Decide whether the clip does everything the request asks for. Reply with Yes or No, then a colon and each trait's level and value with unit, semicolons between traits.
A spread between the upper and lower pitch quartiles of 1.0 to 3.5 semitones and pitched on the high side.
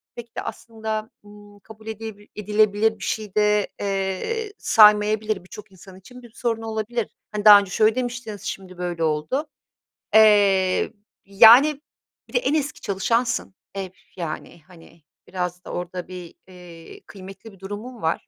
Yes: average, 2.9 semitones; high, 210 Hz